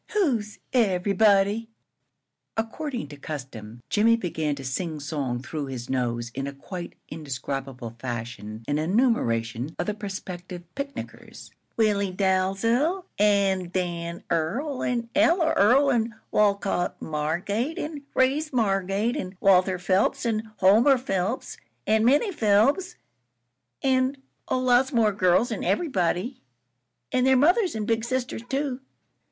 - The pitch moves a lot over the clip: Yes, wide, 7.2 semitones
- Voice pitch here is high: Yes, high, 200 Hz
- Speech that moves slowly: Yes, slow, 125 wpm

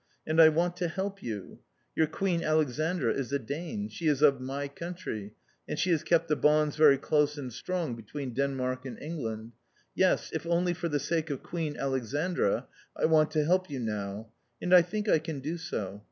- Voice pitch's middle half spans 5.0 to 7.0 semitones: No, average, 4.3 semitones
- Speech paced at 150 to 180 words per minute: No, average, 195 wpm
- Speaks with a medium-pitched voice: Yes, medium, 150 Hz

